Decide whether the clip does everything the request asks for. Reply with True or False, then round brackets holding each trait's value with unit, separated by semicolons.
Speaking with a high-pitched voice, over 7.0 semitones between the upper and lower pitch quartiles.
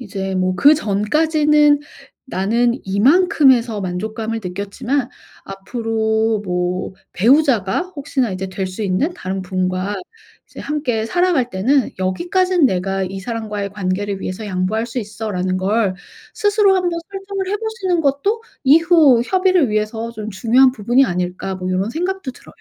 True (225 Hz; 7.4 semitones)